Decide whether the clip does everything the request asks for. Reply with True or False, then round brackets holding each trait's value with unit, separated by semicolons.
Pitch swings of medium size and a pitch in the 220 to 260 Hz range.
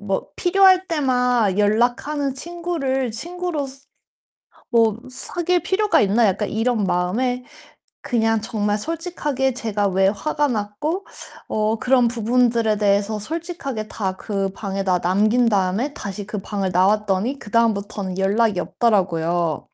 True (5.0 semitones; 225 Hz)